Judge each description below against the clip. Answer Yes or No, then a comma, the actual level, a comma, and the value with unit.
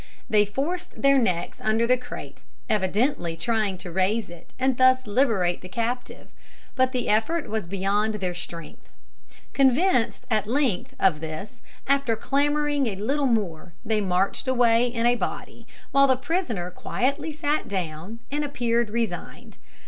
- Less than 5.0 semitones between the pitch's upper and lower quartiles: No, wide, 5.5 semitones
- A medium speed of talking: Yes, average, 150 wpm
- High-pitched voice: Yes, high, 230 Hz